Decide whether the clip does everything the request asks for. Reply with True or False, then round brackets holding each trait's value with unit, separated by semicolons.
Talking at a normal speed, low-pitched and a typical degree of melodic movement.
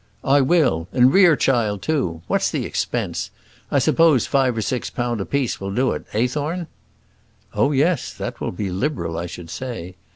False (170 wpm; 125 Hz; 6.4 semitones)